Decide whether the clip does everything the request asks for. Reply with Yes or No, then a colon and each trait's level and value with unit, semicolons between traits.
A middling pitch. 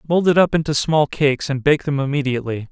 Yes: medium, 145 Hz